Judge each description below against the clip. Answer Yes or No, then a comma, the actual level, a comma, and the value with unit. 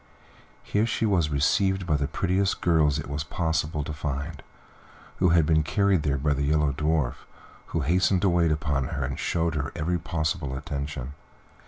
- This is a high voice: No, very low, 75 Hz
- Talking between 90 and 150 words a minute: No, average, 175 wpm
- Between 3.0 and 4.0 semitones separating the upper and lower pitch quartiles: Yes, average, 3.3 semitones